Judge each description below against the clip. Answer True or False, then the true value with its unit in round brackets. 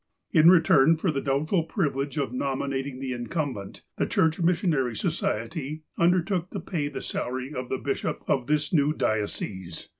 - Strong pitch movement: False (3.8 semitones)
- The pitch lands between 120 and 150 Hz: True (140 Hz)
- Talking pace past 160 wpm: False (155 wpm)